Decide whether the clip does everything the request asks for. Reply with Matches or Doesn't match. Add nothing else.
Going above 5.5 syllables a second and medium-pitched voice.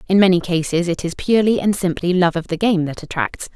Matches